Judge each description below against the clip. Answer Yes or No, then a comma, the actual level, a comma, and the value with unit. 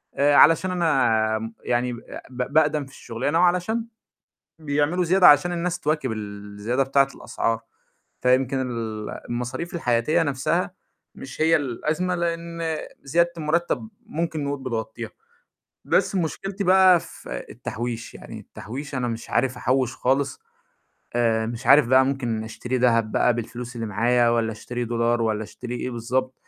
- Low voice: Yes, low, 130 Hz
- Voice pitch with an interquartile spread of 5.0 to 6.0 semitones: Yes, average, 5.3 semitones